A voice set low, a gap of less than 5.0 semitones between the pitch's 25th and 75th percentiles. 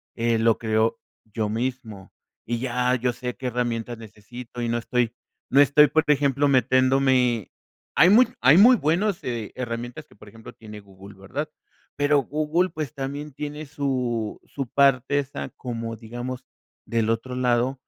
Yes: low, 125 Hz; average, 3.6 semitones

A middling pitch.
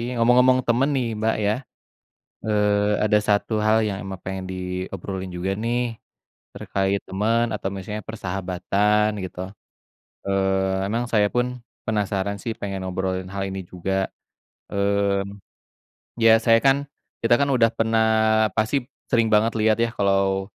No: low, 100 Hz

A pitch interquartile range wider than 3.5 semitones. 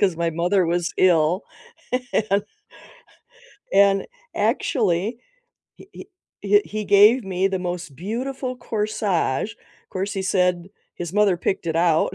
No: average, 3.1 semitones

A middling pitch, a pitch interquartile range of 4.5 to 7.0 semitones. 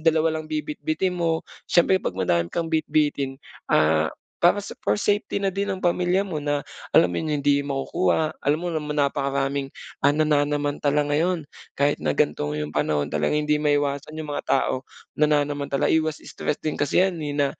No: medium, 150 Hz; average, 2.7 semitones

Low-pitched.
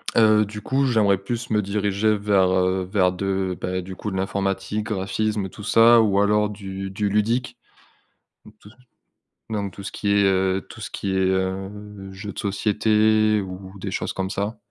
Yes: low, 100 Hz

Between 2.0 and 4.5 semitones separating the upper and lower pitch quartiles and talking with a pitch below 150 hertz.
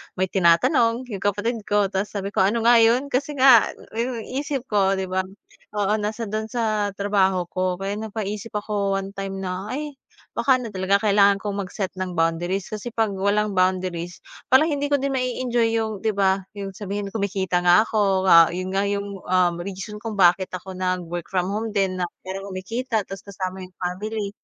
No: average, 2.8 semitones; high, 200 Hz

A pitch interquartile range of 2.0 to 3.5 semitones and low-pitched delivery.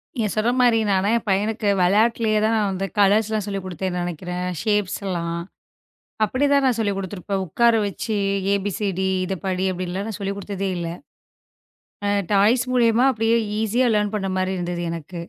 No: average, 2.8 semitones; high, 200 Hz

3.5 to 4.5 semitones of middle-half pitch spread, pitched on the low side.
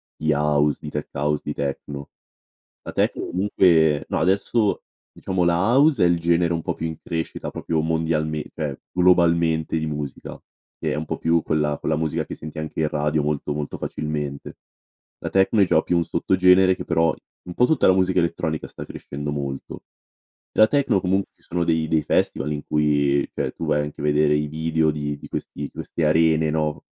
No: narrow, 2.5 semitones; very low, 80 Hz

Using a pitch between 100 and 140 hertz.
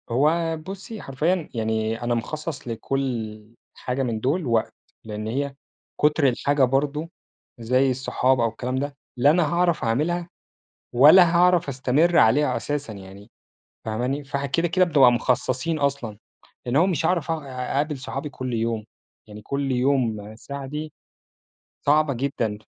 Yes: low, 135 Hz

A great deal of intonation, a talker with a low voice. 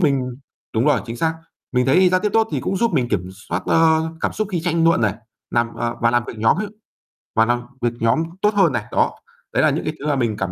Yes: wide, 6.3 semitones; low, 130 Hz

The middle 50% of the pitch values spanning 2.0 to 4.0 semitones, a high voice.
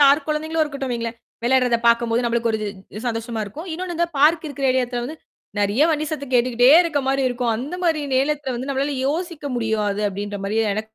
No: average, 4.5 semitones; very high, 260 Hz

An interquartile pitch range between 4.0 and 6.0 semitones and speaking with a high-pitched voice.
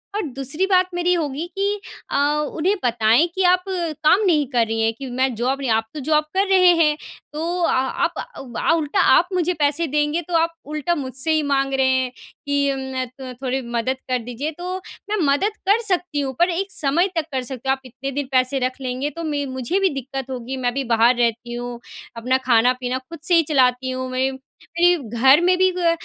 Yes: average, 4.8 semitones; very high, 280 Hz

